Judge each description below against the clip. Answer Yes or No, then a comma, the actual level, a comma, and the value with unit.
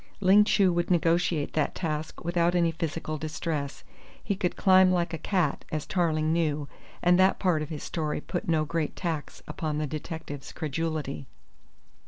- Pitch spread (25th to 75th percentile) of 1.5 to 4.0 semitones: Yes, narrow, 2.4 semitones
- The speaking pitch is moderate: Yes, medium, 165 Hz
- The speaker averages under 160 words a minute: No, average, 165 wpm